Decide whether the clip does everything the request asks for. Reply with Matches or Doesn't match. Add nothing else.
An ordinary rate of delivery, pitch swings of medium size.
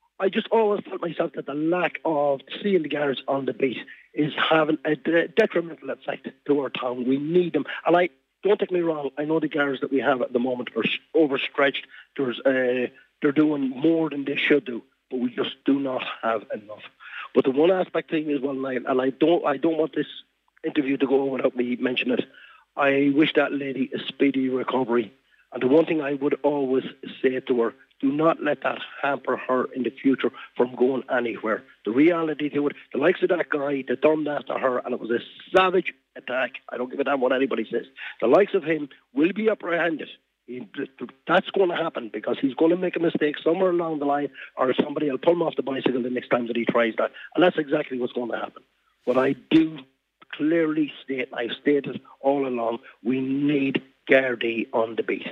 Doesn't match